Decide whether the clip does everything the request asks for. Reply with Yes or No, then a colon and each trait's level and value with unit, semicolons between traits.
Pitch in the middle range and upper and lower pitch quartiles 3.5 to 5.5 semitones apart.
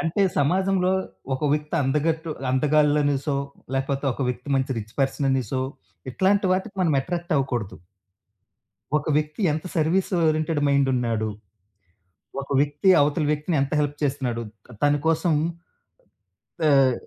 No: medium, 145 Hz; average, 3.0 semitones